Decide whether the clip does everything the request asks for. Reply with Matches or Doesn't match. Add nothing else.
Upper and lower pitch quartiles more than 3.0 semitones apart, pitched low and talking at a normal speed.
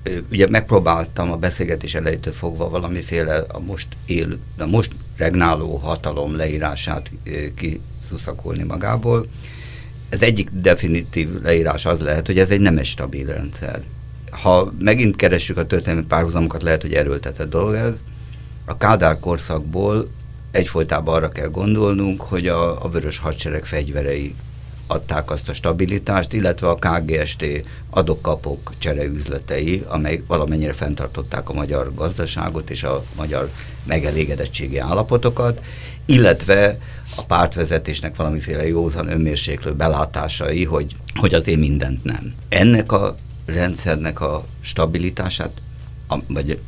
Matches